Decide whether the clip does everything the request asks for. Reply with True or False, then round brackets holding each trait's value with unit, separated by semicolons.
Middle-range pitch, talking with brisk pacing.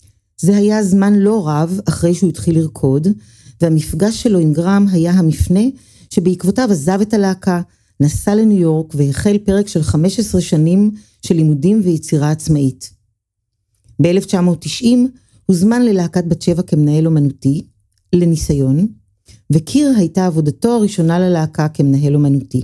False (170 Hz; 120 wpm)